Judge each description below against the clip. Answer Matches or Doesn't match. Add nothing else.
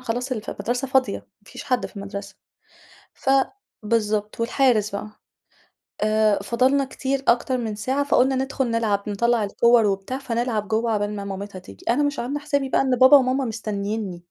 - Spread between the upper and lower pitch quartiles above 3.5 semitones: Matches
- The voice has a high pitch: Matches